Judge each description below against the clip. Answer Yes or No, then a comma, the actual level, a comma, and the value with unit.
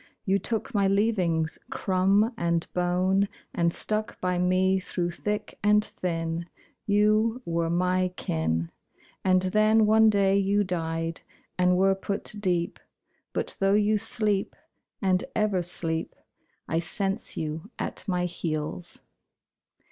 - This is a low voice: No, medium, 185 Hz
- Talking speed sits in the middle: No, slow, 125 wpm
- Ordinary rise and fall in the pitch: Yes, average, 3.3 semitones